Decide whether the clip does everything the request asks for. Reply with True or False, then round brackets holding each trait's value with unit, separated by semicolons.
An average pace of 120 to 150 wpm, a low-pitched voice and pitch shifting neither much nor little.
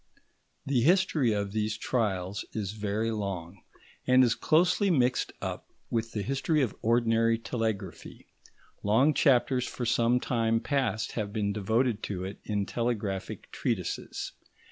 True (135 wpm; 115 Hz; 3.4 semitones)